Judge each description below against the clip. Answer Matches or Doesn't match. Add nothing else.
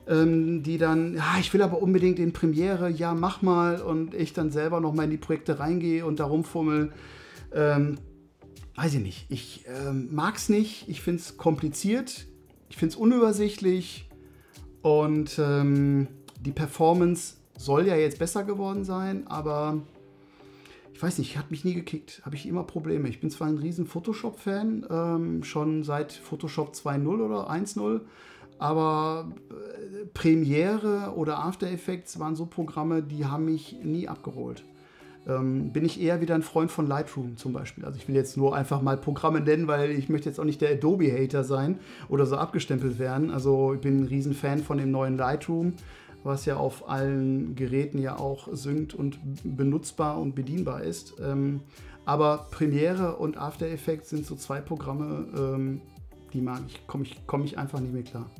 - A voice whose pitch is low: Doesn't match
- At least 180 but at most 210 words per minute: Doesn't match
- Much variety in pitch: Doesn't match